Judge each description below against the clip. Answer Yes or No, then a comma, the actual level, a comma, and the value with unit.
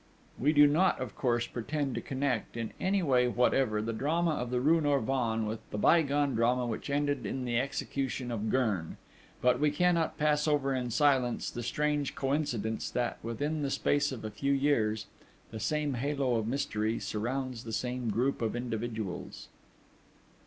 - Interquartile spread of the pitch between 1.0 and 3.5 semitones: No, average, 3.9 semitones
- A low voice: Yes, low, 130 Hz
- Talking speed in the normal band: Yes, average, 170 wpm